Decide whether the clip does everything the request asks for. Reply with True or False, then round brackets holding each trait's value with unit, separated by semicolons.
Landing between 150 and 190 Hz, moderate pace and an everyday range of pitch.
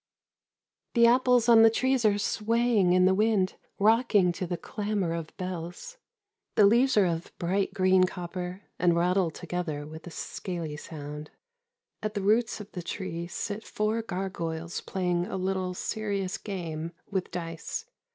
True (185 Hz; 150 wpm; 3.7 semitones)